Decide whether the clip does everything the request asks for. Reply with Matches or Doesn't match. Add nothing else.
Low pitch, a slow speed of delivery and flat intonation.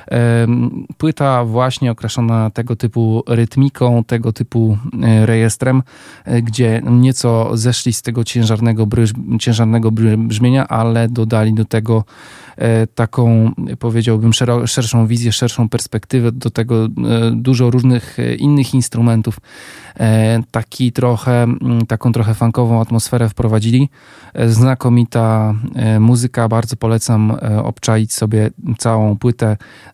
Matches